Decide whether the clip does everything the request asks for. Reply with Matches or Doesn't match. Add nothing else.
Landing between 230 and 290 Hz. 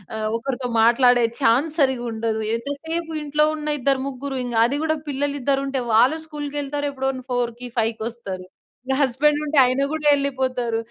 Matches